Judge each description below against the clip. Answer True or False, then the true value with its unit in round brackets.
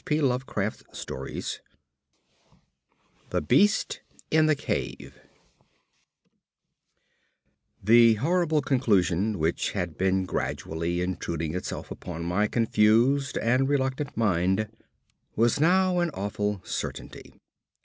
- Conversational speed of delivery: False (90 wpm)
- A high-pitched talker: False (110 Hz)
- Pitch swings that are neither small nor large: False (6.9 semitones)